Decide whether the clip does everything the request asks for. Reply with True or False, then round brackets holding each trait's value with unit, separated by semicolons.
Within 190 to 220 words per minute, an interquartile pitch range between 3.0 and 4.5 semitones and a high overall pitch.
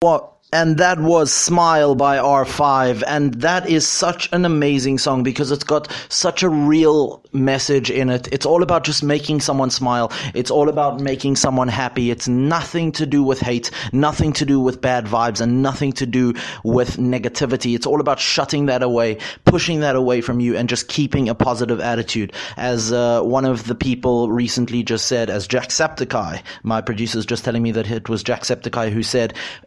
False (205 wpm; 3.5 semitones; 130 Hz)